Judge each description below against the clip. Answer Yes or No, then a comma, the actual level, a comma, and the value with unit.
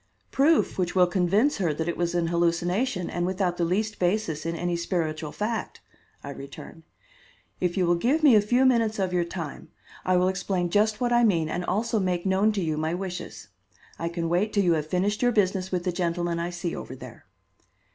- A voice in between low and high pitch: Yes, medium, 180 Hz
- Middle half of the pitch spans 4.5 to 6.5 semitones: No, average, 3.3 semitones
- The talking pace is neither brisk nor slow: No, fast, 210 wpm